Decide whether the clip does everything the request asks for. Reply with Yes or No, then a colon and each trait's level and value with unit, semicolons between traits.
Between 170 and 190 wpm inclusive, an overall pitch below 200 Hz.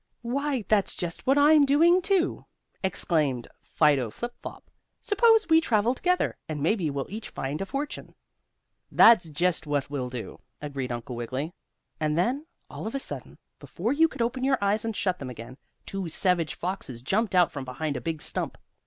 Yes: average, 180 wpm; medium, 185 Hz